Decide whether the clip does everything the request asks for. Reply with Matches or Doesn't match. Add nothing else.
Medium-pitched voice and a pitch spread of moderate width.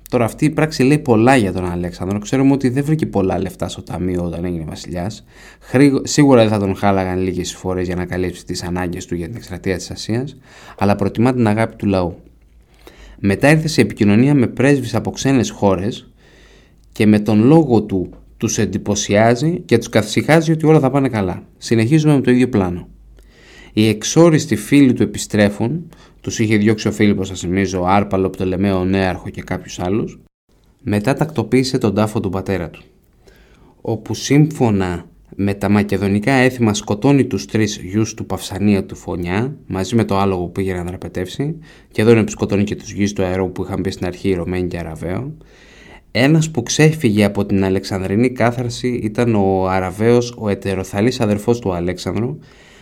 Doesn't match